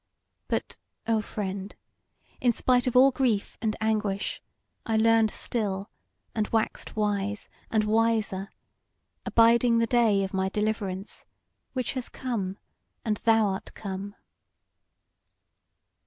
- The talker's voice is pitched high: Yes, high, 215 Hz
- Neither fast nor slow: No, slow, 115 wpm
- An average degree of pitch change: No, narrow, 2.3 semitones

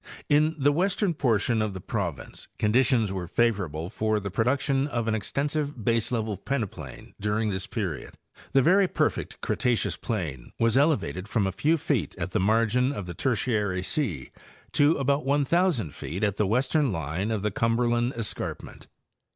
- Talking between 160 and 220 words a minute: Yes, average, 165 wpm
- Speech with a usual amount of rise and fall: No, wide, 5.8 semitones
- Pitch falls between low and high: No, low, 115 Hz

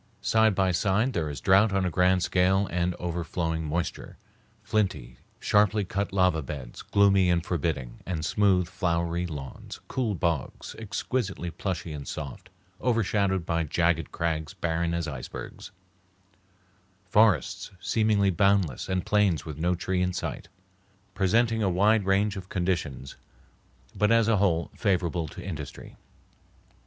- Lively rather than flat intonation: No, average, 3.3 semitones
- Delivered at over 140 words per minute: No, slow, 135 wpm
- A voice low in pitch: Yes, very low, 90 Hz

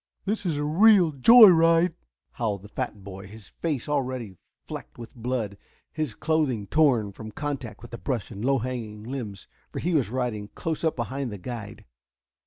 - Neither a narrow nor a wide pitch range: No, wide, 6.0 semitones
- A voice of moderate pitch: No, low, 125 Hz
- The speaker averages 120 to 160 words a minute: No, average, 175 wpm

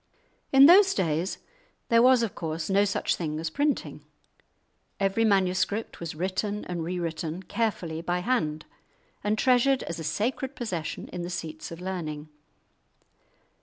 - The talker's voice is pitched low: No, medium, 185 Hz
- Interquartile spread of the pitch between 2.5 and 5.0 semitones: No, wide, 5.5 semitones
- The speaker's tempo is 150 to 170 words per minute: No, average, 140 wpm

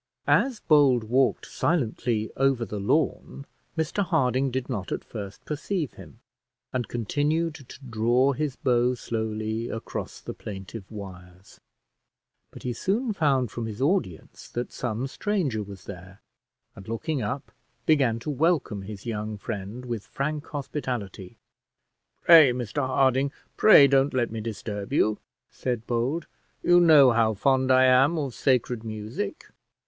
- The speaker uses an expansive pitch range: No, average, 4.5 semitones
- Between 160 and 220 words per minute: No, average, 140 wpm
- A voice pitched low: Yes, low, 125 Hz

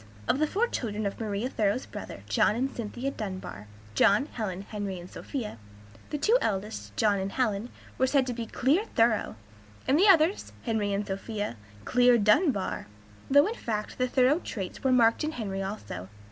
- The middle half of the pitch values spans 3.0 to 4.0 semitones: No, average, 4.7 semitones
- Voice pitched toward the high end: Yes, high, 225 Hz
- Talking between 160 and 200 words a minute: Yes, average, 175 wpm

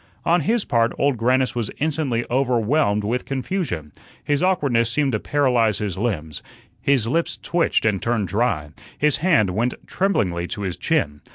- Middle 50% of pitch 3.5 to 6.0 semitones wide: Yes, wide, 5.5 semitones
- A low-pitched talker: Yes, low, 120 Hz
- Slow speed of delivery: No, average, 160 wpm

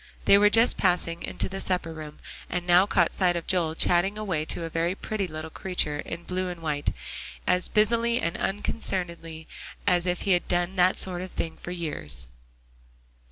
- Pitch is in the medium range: Yes, medium, 175 Hz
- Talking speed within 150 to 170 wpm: No, average, 185 wpm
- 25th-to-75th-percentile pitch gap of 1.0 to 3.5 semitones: Yes, narrow, 2.4 semitones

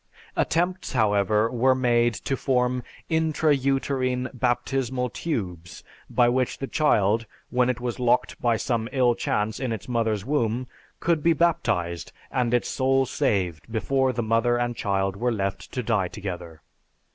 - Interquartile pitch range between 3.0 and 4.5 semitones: Yes, average, 3.3 semitones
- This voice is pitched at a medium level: No, low, 120 Hz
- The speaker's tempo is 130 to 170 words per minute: Yes, average, 150 wpm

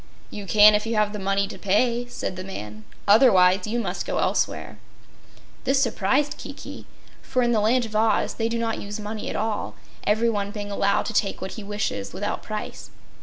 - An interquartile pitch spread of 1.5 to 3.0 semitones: Yes, narrow, 2.5 semitones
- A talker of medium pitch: No, high, 210 Hz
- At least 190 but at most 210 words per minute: Yes, average, 195 wpm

